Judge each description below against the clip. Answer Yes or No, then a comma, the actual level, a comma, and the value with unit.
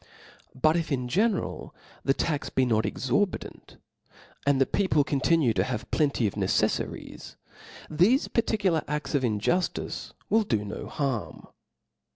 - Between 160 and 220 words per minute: No, average, 140 wpm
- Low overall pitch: No, medium, 145 Hz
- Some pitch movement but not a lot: No, wide, 5.7 semitones